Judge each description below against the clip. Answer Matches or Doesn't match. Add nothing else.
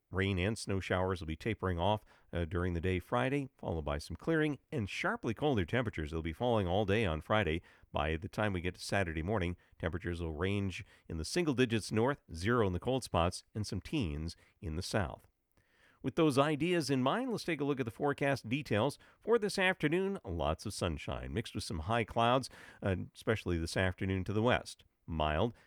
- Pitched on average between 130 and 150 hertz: Doesn't match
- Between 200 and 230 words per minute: Matches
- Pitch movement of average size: Doesn't match